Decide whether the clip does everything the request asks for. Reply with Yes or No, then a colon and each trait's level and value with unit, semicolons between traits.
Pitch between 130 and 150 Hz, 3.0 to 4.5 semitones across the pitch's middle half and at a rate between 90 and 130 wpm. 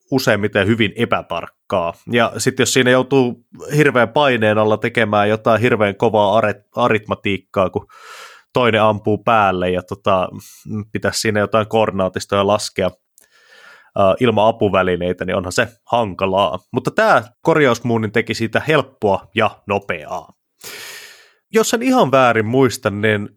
No: low, 110 Hz; average, 3.5 semitones; average, 125 wpm